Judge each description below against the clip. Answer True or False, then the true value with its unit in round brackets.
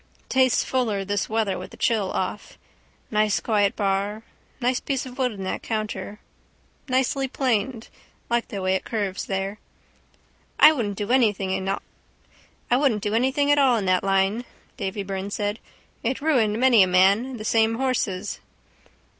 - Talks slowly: False (145 wpm)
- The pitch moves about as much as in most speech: True (4.1 semitones)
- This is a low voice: False (215 Hz)